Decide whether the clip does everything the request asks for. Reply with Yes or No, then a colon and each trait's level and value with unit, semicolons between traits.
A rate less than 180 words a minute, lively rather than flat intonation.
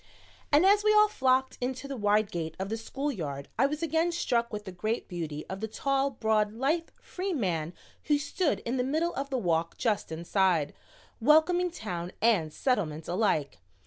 No: average, 185 wpm; wide, 8.0 semitones